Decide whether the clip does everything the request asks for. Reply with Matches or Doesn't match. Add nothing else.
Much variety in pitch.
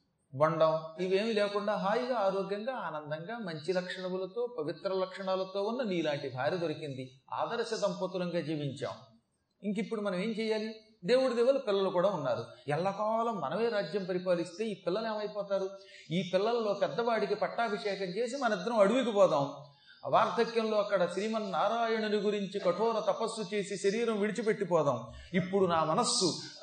Doesn't match